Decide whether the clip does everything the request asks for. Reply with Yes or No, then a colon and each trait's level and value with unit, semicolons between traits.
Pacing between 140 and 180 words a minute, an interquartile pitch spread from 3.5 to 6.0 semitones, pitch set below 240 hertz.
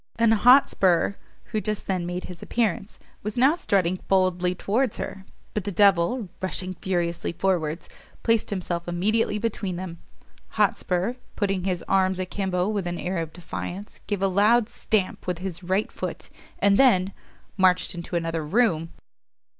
No: average, 155 wpm; average, 2.8 semitones; high, 190 Hz